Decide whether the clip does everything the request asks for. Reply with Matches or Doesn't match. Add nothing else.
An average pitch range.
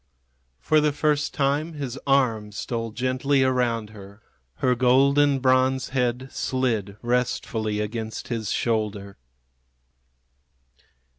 Matches